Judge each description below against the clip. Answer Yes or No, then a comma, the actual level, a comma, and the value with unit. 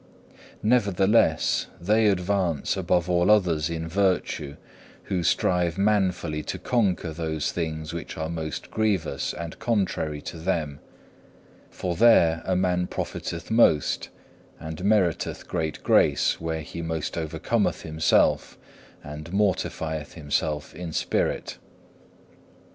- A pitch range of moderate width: Yes, average, 3.2 semitones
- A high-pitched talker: No, very low, 85 Hz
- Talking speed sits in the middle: No, slow, 115 wpm